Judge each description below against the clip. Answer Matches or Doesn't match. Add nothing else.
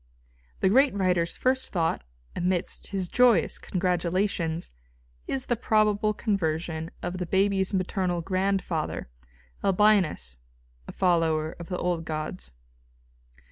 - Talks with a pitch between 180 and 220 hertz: Matches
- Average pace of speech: Doesn't match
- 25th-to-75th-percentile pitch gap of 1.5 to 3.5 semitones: Matches